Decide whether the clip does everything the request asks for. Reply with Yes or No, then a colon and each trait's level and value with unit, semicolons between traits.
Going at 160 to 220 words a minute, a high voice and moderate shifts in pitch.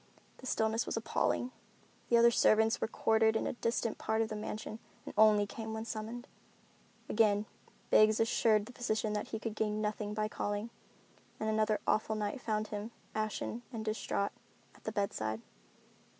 No: average, 165 wpm; high, 220 Hz; narrow, 1.0 semitones